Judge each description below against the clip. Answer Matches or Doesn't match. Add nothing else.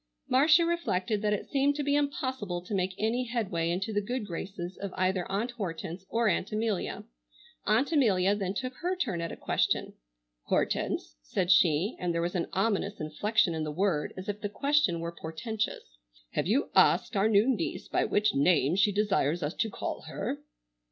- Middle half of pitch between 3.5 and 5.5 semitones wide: Matches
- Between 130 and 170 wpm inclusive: Doesn't match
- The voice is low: Doesn't match